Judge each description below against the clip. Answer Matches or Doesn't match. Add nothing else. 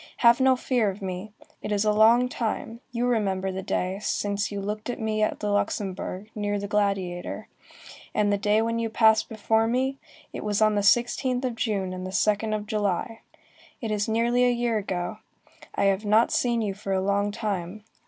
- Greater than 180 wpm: Matches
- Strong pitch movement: Doesn't match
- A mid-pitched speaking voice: Doesn't match